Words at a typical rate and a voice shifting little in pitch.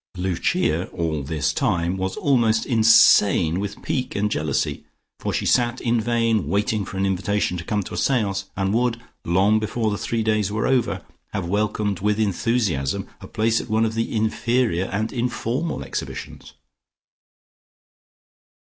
No: average, 155 wpm; average, 3.2 semitones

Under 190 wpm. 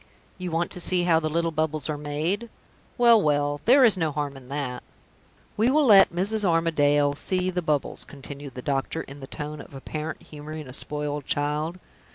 No: average, 195 wpm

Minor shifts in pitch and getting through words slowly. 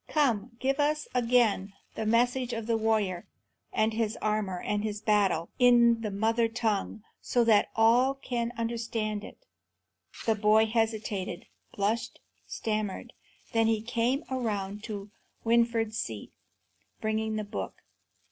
Yes: narrow, 2.0 semitones; slow, 130 wpm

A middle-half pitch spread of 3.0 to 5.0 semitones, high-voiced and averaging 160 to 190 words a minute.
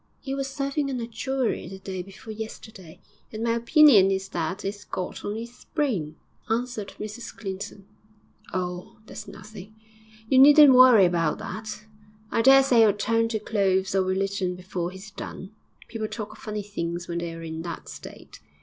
Yes: average, 3.8 semitones; high, 210 Hz; average, 165 wpm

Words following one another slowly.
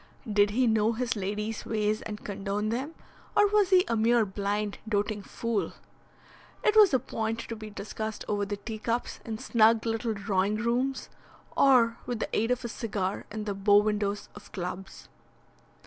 No: average, 170 wpm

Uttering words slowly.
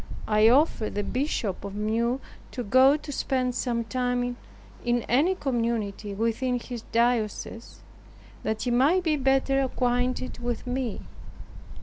Yes: slow, 130 wpm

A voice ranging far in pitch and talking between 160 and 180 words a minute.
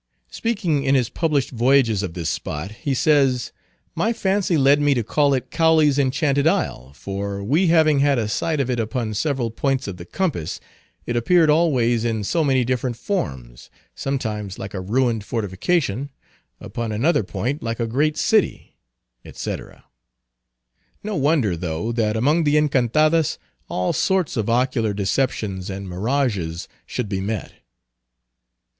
No: wide, 5.8 semitones; average, 150 wpm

